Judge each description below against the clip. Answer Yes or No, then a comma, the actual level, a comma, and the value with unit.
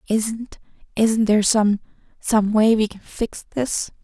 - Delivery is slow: Yes, slow, 120 wpm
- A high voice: Yes, high, 215 Hz